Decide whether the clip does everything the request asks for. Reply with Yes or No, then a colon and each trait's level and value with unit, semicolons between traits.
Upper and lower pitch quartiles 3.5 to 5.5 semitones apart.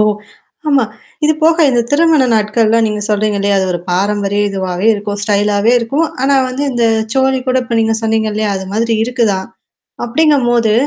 Yes: average, 3.8 semitones